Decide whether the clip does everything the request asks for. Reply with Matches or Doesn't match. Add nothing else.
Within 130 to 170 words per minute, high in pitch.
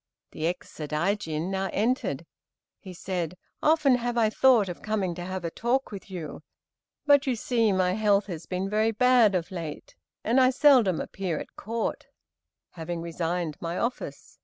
Matches